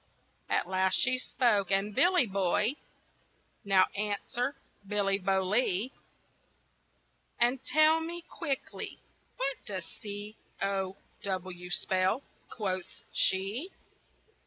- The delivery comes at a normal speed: No, slow, 95 wpm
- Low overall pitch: No, high, 205 Hz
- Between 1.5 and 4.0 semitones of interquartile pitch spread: No, average, 5.0 semitones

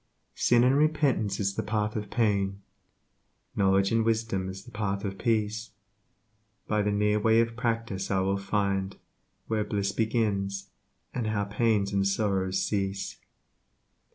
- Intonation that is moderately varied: No, narrow, 2.3 semitones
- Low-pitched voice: Yes, low, 105 Hz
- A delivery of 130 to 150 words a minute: Yes, average, 140 wpm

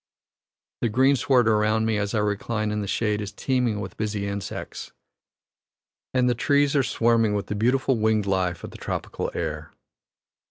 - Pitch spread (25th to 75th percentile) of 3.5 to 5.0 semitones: No, average, 2.9 semitones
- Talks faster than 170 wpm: No, average, 165 wpm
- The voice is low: Yes, low, 110 Hz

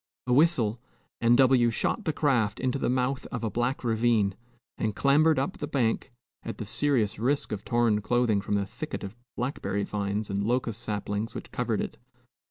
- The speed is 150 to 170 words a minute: No, average, 180 wpm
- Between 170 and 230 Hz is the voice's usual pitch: No, low, 120 Hz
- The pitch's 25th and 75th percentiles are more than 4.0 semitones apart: No, average, 3.7 semitones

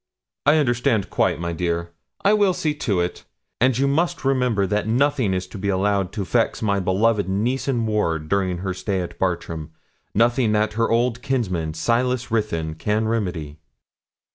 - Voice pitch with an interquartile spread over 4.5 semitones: Yes, average, 4.9 semitones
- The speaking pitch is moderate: No, low, 105 Hz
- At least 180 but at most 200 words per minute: No, average, 170 wpm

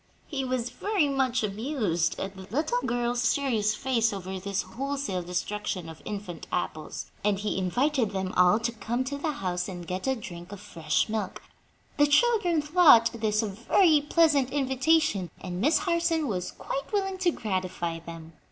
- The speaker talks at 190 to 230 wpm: No, average, 170 wpm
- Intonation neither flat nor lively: No, wide, 7.2 semitones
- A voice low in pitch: No, high, 230 Hz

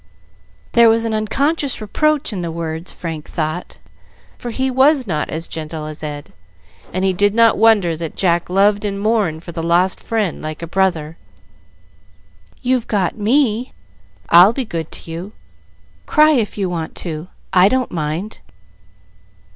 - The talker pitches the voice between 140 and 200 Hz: Yes, high, 190 Hz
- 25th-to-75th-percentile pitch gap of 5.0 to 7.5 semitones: Yes, wide, 5.5 semitones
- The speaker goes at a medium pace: Yes, average, 155 wpm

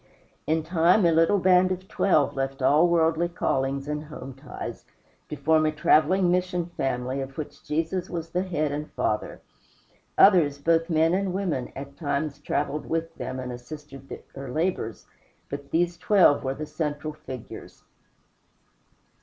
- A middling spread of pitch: Yes, average, 3.7 semitones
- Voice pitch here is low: No, medium, 155 Hz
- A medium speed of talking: Yes, average, 155 wpm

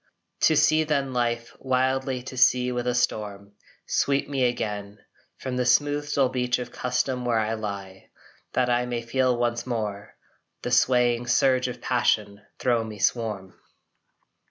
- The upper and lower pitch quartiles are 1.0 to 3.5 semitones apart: Yes, narrow, 2.4 semitones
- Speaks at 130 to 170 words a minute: Yes, average, 155 wpm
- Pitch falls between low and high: No, low, 125 Hz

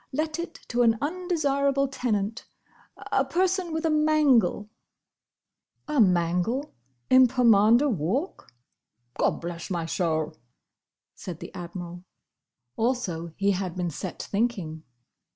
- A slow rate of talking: Yes, slow, 100 wpm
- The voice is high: Yes, high, 230 Hz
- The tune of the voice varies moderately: No, wide, 8.0 semitones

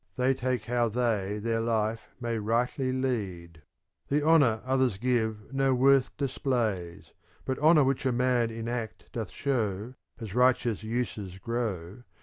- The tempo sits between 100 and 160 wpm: Yes, average, 145 wpm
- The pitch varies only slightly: No, average, 3.1 semitones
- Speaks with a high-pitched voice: No, low, 120 Hz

